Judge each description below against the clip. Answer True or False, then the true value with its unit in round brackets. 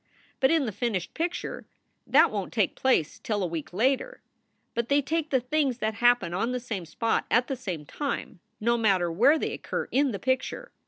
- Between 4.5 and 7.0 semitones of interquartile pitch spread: True (5.4 semitones)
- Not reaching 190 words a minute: False (205 wpm)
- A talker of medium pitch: False (240 Hz)